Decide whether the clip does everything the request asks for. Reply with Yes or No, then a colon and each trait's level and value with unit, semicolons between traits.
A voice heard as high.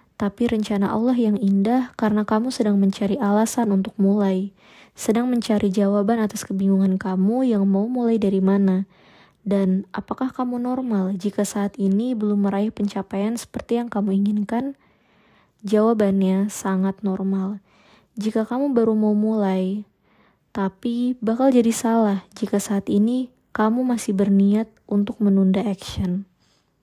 Yes: high, 205 Hz